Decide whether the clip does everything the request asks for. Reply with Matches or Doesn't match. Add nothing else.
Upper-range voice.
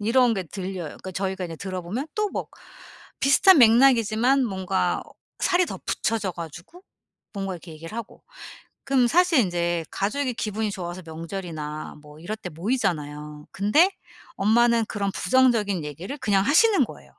Matches